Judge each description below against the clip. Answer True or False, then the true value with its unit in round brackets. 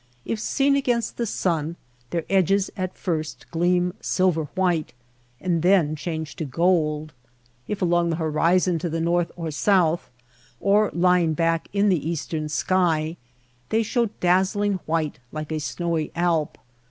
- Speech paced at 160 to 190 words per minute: False (145 wpm)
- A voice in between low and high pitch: True (170 Hz)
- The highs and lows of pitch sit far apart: False (2.8 semitones)